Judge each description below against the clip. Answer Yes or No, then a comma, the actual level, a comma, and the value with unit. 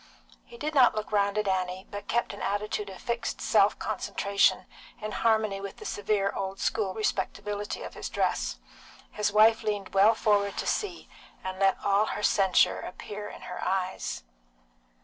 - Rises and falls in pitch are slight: Yes, narrow, 1.7 semitones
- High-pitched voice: Yes, high, 205 Hz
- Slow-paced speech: No, average, 170 wpm